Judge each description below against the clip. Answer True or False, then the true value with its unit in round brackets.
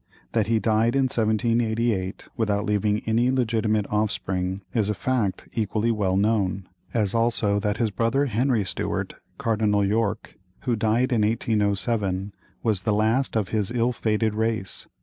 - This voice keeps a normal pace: True (150 wpm)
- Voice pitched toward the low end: True (110 Hz)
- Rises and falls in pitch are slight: True (2.0 semitones)